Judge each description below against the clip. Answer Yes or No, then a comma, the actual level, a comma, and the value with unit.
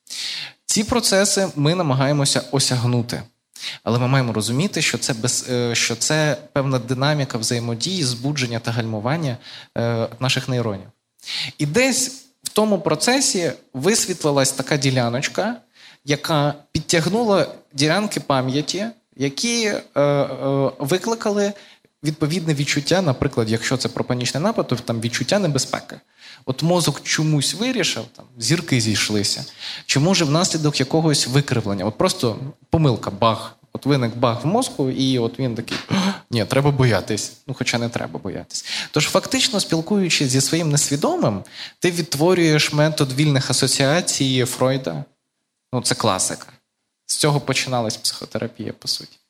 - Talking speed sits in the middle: Yes, average, 125 wpm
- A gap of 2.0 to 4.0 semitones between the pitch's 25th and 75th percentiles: No, average, 4.9 semitones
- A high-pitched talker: No, medium, 140 Hz